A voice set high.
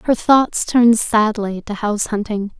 Yes: high, 215 Hz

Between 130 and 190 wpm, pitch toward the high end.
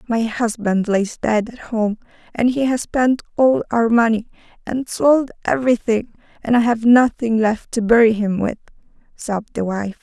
Yes: average, 170 wpm; high, 230 Hz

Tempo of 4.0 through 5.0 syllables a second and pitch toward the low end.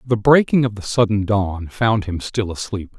Yes: 4.5 syllables/s; low, 105 Hz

